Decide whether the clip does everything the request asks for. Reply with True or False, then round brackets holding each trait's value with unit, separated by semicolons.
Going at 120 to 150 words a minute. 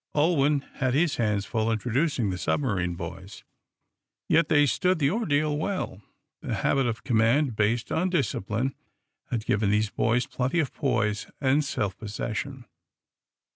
True (140 wpm)